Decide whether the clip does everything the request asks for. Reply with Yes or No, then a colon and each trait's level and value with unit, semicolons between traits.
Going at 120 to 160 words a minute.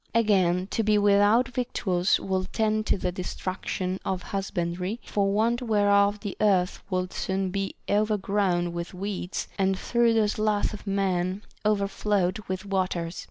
Yes: average, 145 wpm